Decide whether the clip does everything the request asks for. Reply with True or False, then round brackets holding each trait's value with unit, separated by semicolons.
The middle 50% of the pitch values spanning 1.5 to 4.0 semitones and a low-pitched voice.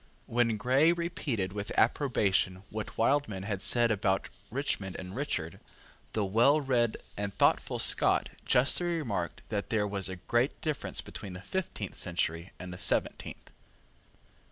False (5.6 semitones; 110 Hz)